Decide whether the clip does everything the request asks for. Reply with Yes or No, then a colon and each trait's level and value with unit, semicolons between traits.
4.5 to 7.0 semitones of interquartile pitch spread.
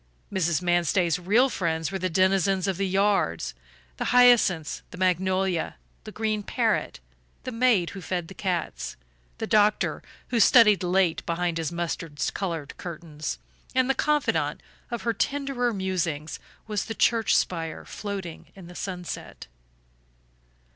No: average, 3.8 semitones